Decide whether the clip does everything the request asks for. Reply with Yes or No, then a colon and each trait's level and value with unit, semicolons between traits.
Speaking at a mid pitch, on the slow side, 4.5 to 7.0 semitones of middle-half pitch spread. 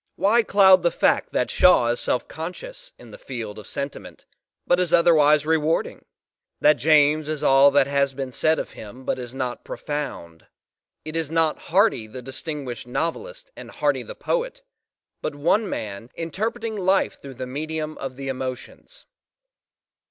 No: medium, 150 Hz; average, 160 wpm; average, 5.2 semitones